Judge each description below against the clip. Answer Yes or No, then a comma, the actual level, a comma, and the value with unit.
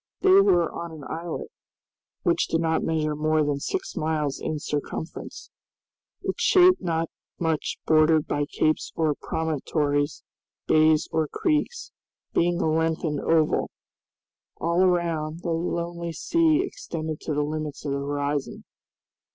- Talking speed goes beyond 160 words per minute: No, slow, 135 wpm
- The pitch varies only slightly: Yes, narrow, 2.0 semitones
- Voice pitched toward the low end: No, medium, 160 Hz